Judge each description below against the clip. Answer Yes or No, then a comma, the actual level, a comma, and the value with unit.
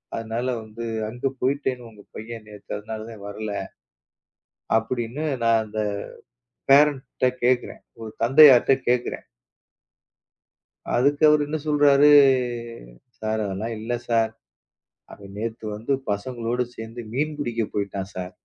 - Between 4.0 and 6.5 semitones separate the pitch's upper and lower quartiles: No, average, 3.2 semitones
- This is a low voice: Yes, low, 115 Hz